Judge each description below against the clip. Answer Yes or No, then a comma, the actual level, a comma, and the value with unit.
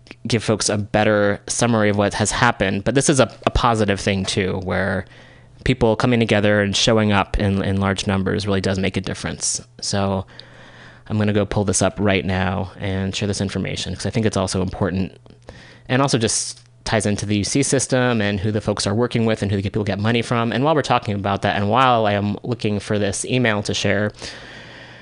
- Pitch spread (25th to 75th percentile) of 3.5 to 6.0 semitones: No, average, 2.8 semitones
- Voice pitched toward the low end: Yes, low, 105 Hz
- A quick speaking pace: Yes, fast, 220 wpm